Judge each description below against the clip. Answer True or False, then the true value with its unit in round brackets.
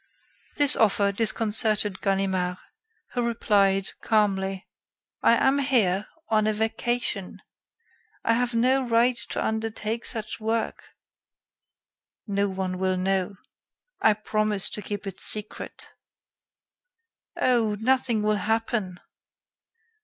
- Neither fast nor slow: False (105 wpm)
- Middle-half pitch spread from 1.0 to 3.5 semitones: True (2.7 semitones)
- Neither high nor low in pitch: False (215 Hz)